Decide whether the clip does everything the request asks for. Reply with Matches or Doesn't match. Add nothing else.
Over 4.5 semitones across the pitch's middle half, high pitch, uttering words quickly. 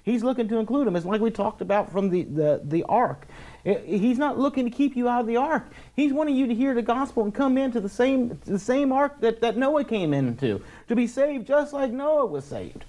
Matches